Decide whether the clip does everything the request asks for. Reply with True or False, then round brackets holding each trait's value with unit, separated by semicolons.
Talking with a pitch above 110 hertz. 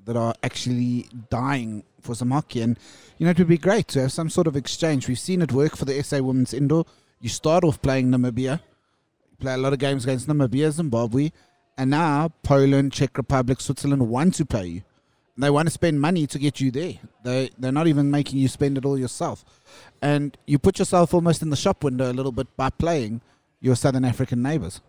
True (140 Hz)